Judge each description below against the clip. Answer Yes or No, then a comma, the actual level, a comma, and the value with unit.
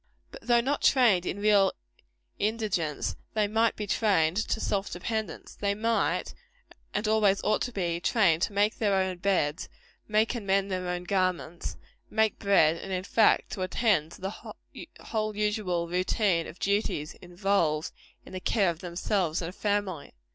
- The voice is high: Yes, high, 195 Hz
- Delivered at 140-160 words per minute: No, average, 170 wpm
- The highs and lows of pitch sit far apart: No, average, 3.2 semitones